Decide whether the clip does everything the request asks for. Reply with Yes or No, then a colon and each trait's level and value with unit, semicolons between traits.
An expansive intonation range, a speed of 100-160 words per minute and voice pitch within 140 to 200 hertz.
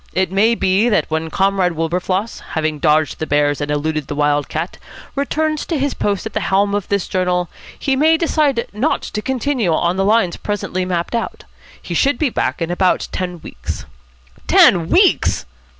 No: wide, 6.1 semitones; average, 185 wpm; high, 190 Hz